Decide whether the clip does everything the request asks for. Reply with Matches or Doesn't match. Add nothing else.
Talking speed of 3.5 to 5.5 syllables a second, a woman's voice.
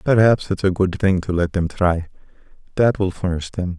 Doesn't match